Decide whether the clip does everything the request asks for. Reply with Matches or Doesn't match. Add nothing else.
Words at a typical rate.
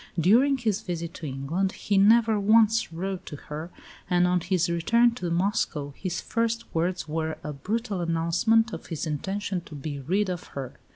Matches